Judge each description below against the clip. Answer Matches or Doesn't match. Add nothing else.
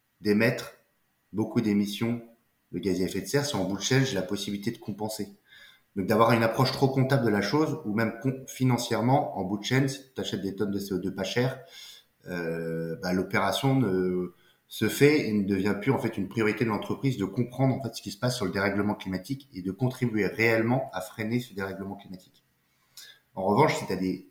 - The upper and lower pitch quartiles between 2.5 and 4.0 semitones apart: Doesn't match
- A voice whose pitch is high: Doesn't match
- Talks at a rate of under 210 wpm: Doesn't match